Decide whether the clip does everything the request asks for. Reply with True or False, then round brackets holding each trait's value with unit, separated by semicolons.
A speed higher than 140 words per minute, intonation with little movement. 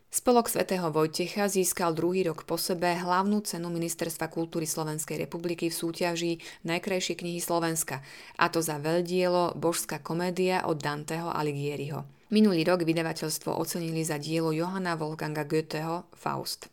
False (135 wpm; 1.8 semitones)